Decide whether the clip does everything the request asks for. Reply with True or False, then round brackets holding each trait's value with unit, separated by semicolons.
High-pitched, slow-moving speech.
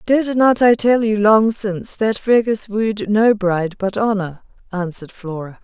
False (210 Hz; 170 wpm)